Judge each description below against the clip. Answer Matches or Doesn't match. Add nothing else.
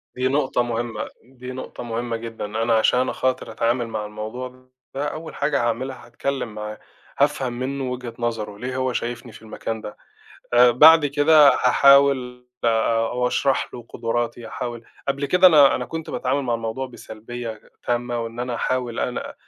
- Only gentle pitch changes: Matches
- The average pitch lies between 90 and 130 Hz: Matches